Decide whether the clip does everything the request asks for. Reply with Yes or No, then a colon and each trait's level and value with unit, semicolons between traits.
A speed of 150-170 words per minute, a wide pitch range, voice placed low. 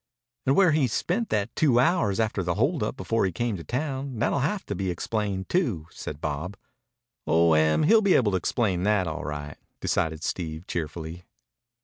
No: average, 190 wpm; wide, 8.1 semitones; low, 100 Hz